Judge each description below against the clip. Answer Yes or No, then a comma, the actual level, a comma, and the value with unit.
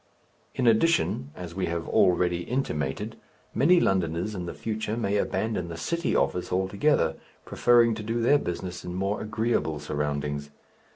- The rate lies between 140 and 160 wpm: Yes, average, 150 wpm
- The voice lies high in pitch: No, very low, 95 Hz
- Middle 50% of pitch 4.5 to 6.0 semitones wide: Yes, wide, 5.4 semitones